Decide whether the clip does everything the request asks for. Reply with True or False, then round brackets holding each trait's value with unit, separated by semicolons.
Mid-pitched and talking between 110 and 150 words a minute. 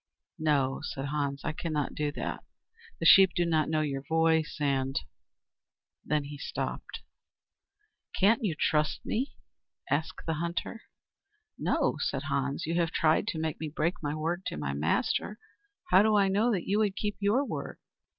False (160 Hz; 170 wpm)